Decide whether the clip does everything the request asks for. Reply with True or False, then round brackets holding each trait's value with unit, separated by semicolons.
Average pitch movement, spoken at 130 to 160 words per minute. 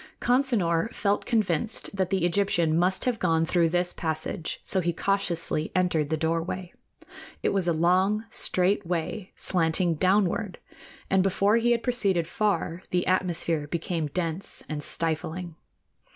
True (3.1 semitones; 140 wpm)